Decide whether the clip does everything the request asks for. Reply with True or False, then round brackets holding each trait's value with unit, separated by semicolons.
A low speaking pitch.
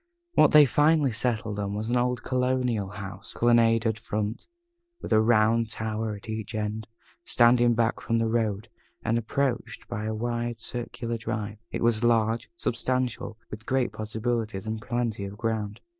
True (115 Hz)